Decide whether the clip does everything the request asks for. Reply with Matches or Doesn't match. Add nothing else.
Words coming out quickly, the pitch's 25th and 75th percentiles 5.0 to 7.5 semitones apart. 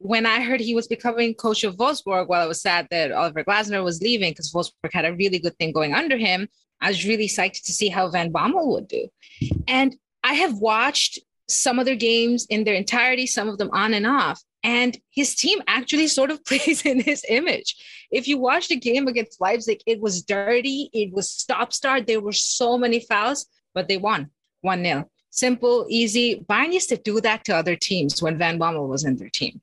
Matches